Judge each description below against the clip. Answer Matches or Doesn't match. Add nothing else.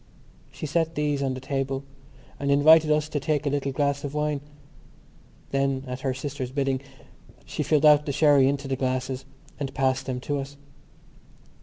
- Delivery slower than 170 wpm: Doesn't match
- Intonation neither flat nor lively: Doesn't match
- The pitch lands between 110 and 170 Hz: Matches